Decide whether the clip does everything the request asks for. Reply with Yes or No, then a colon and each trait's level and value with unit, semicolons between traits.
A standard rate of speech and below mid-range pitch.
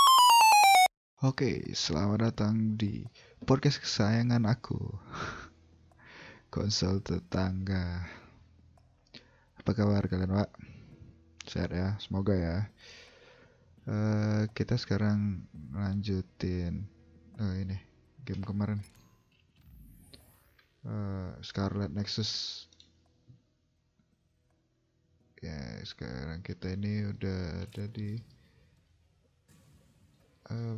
No: slow, 70 wpm; low, 100 Hz